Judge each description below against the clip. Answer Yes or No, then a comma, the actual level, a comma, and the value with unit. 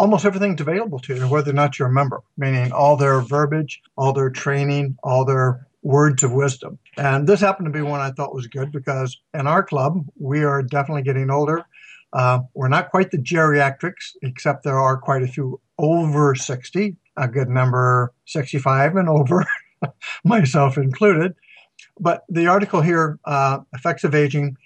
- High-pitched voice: No, medium, 140 Hz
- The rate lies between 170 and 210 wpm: Yes, average, 175 wpm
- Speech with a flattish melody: No, average, 3.1 semitones